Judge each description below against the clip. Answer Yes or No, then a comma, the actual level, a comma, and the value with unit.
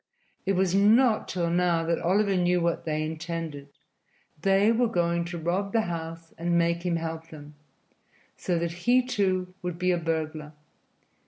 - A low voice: No, medium, 170 Hz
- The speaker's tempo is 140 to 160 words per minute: No, average, 170 wpm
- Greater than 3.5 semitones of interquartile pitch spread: No, narrow, 2.4 semitones